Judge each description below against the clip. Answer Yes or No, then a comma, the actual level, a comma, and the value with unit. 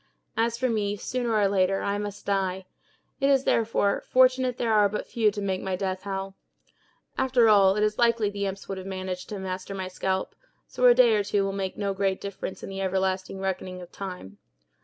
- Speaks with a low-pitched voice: No, high, 200 Hz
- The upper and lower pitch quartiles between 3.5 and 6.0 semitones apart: No, narrow, 2.4 semitones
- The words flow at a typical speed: No, fast, 210 wpm